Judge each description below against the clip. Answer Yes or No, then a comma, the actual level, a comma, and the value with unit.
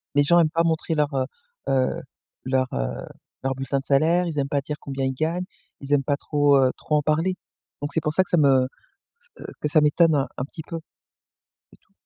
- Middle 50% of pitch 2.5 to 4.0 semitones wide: Yes, average, 2.9 semitones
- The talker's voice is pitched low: No, medium, 145 Hz